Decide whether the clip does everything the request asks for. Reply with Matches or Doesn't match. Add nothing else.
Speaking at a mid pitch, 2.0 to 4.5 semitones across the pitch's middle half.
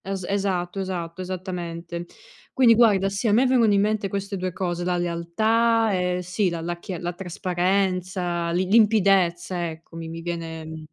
Matches